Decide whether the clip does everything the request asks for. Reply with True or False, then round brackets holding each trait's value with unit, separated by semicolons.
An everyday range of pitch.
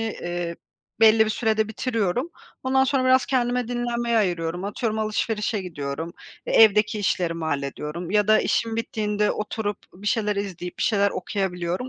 True (4.3 semitones)